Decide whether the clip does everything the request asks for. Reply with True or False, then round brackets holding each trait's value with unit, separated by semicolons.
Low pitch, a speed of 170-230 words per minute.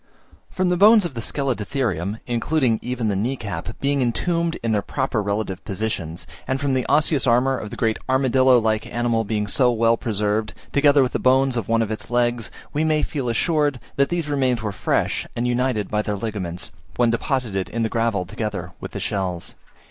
True (120 Hz; 195 wpm)